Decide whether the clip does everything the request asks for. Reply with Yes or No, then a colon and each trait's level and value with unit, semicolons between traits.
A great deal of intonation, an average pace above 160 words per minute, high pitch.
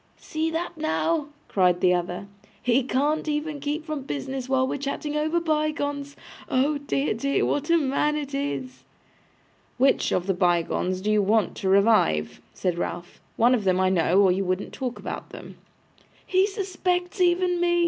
Yes: wide, 7.9 semitones; average, 170 wpm; very high, 275 Hz